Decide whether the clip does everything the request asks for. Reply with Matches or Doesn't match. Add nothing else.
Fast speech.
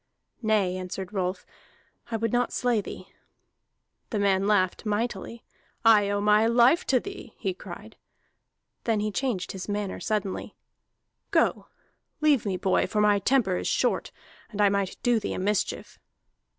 Doesn't match